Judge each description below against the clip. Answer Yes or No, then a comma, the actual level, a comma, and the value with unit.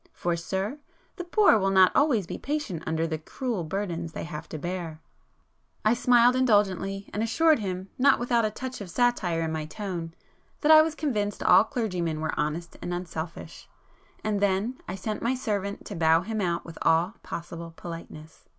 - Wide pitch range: Yes, wide, 5.7 semitones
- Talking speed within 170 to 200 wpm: Yes, average, 180 wpm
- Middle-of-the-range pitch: No, high, 195 Hz